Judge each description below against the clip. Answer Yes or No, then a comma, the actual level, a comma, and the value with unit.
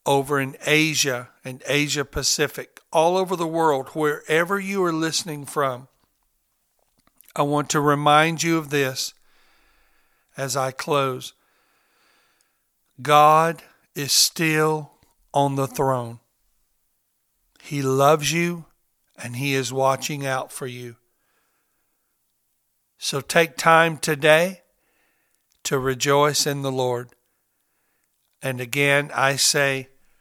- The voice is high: No, medium, 140 Hz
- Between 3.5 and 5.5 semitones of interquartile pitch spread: No, average, 2.7 semitones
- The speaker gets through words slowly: Yes, slow, 105 wpm